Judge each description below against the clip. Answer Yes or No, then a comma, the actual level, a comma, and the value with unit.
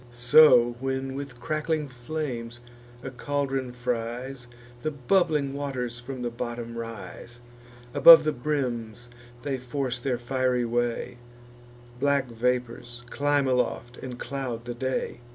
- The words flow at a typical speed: No, slow, 120 wpm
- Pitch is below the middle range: Yes, low, 125 Hz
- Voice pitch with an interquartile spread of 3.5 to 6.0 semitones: No, narrow, 2.4 semitones